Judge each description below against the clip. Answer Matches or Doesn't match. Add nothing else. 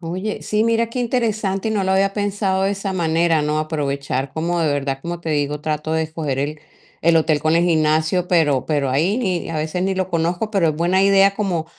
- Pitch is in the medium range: Matches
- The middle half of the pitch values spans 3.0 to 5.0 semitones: Matches